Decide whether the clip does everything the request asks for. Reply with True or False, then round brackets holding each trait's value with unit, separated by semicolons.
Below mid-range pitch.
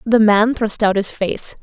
False (215 Hz)